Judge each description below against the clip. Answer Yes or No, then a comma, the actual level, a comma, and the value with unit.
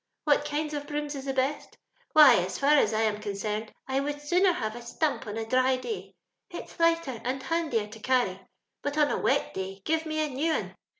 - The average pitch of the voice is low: No, very high, 270 Hz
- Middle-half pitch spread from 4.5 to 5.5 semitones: Yes, average, 5.1 semitones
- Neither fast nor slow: No, fast, 230 wpm